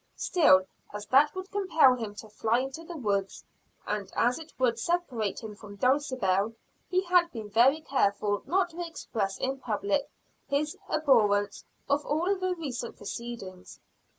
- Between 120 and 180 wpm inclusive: Yes, average, 150 wpm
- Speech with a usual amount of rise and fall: No, wide, 7.1 semitones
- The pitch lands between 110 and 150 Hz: No, very high, 255 Hz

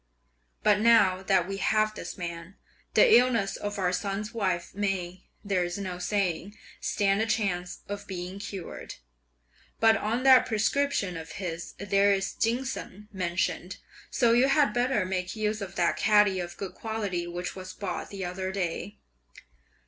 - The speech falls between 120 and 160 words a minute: Yes, average, 155 wpm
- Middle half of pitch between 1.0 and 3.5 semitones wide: Yes, average, 2.8 semitones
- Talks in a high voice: Yes, high, 195 Hz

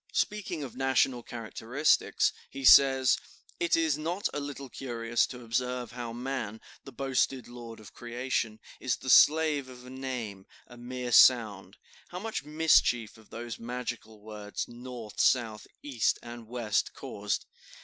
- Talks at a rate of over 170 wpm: No, average, 145 wpm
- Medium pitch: No, low, 125 Hz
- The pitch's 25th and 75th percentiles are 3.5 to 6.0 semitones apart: No, average, 2.7 semitones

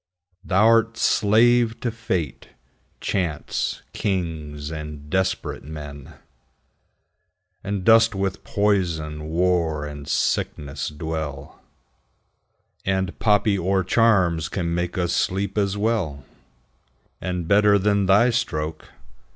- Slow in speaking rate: Yes, slow, 100 wpm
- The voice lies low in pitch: Yes, very low, 90 Hz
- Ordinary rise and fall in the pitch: Yes, average, 4.9 semitones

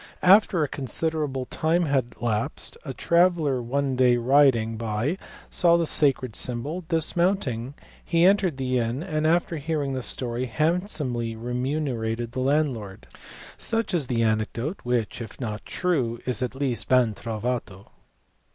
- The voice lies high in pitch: No, low, 130 Hz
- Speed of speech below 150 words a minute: Yes, average, 140 wpm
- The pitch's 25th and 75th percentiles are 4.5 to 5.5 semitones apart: Yes, average, 5.1 semitones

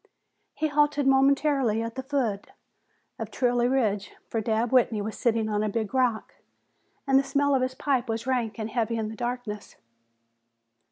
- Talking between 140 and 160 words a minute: No, average, 170 wpm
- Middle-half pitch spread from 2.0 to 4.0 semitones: Yes, average, 3.4 semitones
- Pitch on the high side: Yes, high, 240 Hz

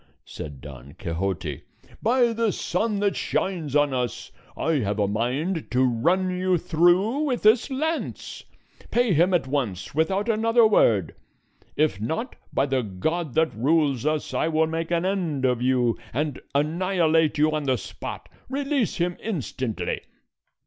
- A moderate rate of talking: Yes, average, 150 wpm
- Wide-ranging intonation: Yes, wide, 7.2 semitones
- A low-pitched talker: No, medium, 160 Hz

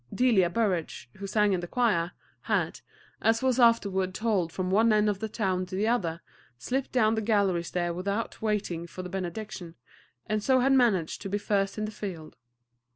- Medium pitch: No, high, 200 Hz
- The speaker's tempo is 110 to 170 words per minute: No, average, 190 wpm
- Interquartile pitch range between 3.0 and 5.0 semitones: Yes, average, 3.4 semitones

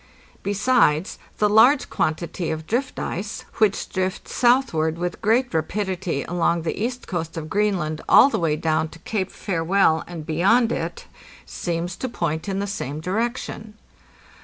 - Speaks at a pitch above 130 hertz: Yes, medium, 185 Hz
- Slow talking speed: No, average, 150 wpm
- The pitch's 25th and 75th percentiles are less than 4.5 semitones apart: No, average, 5.0 semitones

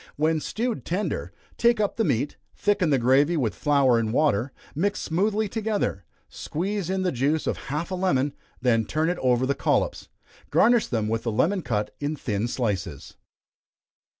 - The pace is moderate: Yes, average, 170 wpm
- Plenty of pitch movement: Yes, wide, 7.8 semitones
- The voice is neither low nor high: Yes, medium, 150 Hz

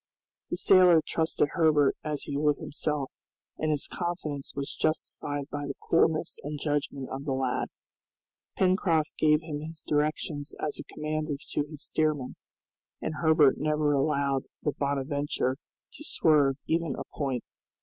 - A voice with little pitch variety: Yes, narrow, 1.8 semitones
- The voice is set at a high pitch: No, medium, 150 Hz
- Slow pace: No, average, 145 wpm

